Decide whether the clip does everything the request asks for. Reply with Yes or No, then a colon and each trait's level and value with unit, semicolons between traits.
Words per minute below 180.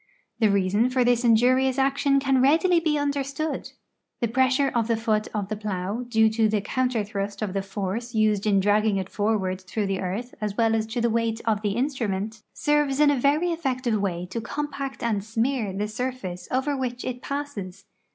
No: average, 195 wpm